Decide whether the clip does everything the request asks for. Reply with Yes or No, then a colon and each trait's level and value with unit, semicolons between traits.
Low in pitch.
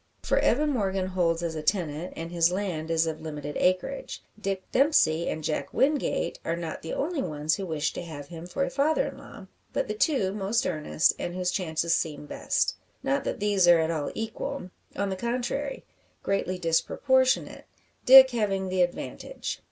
No: medium, 185 Hz